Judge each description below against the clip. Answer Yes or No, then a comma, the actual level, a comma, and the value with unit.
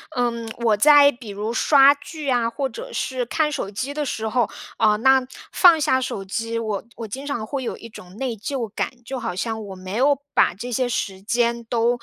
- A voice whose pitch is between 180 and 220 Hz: No, high, 235 Hz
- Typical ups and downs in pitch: Yes, average, 3.7 semitones